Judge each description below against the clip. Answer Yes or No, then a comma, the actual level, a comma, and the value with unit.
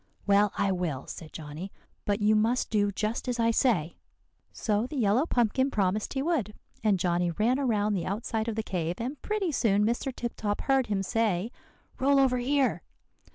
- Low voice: No, high, 215 Hz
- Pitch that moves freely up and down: No, average, 4.1 semitones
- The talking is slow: No, average, 185 wpm